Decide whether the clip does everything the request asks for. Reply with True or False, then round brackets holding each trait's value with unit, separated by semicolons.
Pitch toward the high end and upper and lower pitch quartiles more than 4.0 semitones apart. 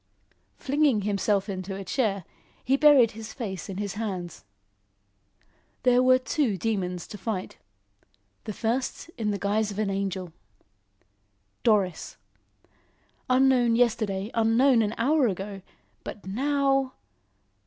True (220 Hz; 4.4 semitones)